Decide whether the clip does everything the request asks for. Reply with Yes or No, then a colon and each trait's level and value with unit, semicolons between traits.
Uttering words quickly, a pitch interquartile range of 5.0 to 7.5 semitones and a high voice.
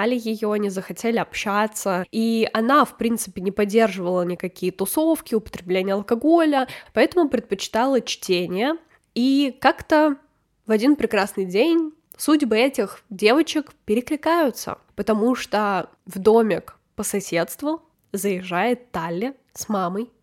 No: slow, 110 wpm; wide, 5.4 semitones; high, 225 Hz